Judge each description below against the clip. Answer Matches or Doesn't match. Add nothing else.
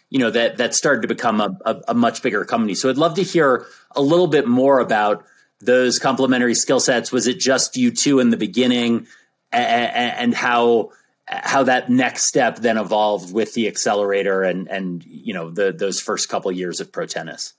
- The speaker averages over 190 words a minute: Matches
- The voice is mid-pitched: Doesn't match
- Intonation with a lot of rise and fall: Doesn't match